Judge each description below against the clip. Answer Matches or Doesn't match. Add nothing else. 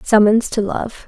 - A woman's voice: Matches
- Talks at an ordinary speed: Matches